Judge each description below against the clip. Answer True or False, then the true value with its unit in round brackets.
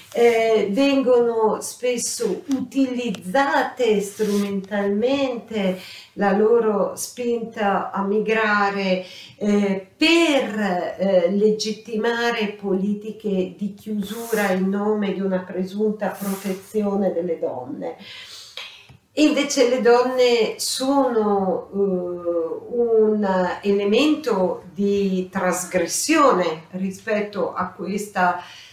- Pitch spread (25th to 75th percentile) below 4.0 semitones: True (3.6 semitones)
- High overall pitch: True (205 Hz)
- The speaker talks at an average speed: False (75 wpm)